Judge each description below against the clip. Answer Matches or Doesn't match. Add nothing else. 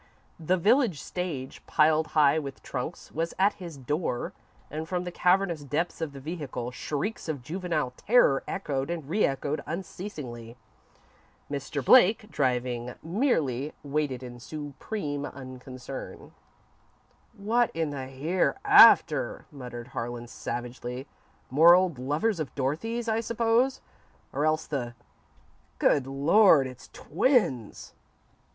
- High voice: Doesn't match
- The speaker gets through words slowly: Matches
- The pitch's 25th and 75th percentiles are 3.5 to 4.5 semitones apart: Doesn't match